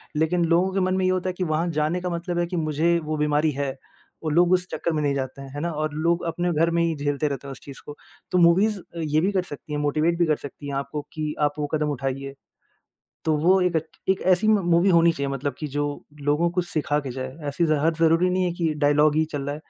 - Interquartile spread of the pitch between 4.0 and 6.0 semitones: No, average, 2.9 semitones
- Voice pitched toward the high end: No, medium, 155 Hz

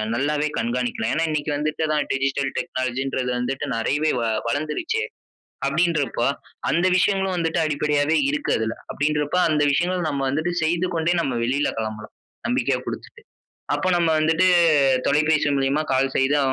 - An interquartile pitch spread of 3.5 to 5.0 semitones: Yes, average, 3.8 semitones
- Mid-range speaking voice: Yes, medium, 150 Hz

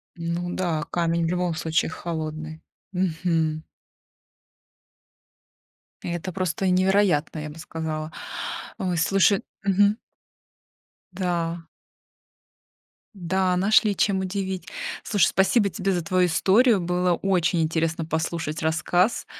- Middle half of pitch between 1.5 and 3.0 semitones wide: Yes, narrow, 2.6 semitones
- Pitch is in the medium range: Yes, medium, 175 Hz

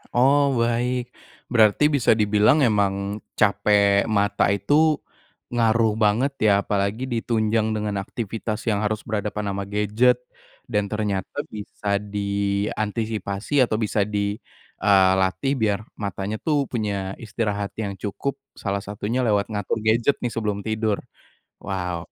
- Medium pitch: No, low, 105 Hz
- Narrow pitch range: Yes, narrow, 2.1 semitones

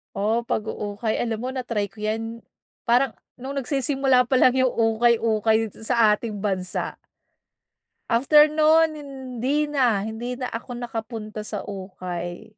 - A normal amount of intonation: Yes, average, 3.3 semitones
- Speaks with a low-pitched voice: No, high, 230 Hz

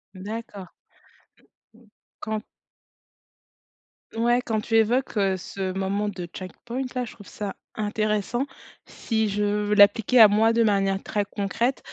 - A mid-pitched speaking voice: No, high, 210 Hz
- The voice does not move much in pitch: Yes, narrow, 2.2 semitones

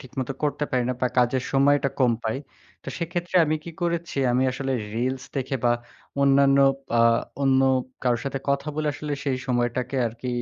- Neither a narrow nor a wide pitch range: No, narrow, 2.2 semitones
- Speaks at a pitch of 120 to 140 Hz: Yes, low, 135 Hz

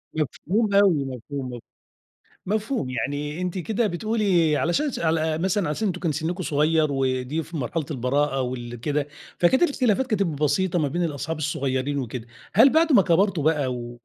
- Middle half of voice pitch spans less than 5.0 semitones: No, average, 5.3 semitones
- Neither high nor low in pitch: Yes, medium, 160 Hz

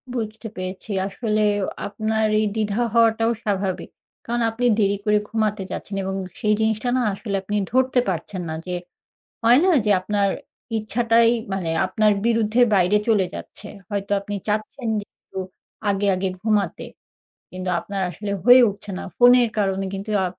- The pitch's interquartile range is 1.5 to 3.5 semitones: Yes, narrow, 2.5 semitones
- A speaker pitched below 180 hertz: No, high, 210 Hz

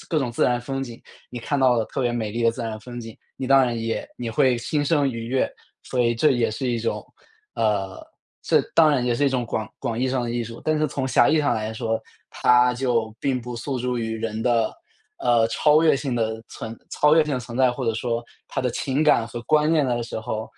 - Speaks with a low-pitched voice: Yes, low, 120 Hz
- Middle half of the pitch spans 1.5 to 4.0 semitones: Yes, average, 2.7 semitones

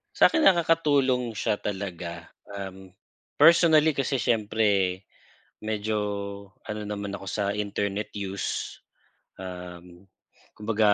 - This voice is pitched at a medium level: No, low, 105 Hz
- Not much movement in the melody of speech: No, average, 4.2 semitones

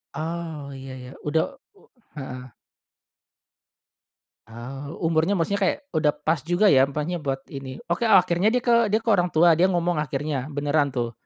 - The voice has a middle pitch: Yes, medium, 155 Hz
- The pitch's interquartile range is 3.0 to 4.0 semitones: No, average, 4.5 semitones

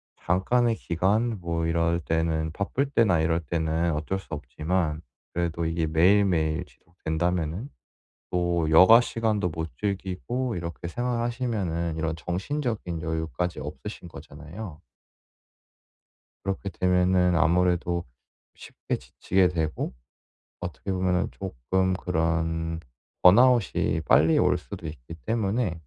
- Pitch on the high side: No, very low, 85 Hz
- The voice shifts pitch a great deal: No, average, 3.1 semitones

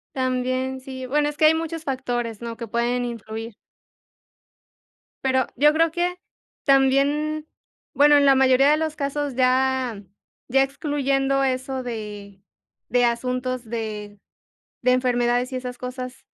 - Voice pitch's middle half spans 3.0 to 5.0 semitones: No, narrow, 2.4 semitones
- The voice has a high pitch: Yes, very high, 260 Hz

